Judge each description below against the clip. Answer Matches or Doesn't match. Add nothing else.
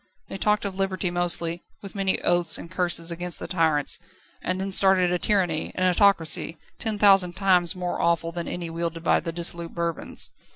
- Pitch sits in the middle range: Matches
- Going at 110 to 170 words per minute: Doesn't match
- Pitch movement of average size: Doesn't match